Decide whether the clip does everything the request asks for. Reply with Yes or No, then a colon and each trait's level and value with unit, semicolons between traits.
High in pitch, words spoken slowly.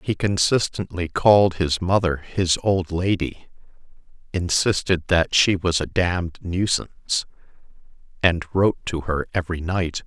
No: very low, 90 Hz; slow, 120 wpm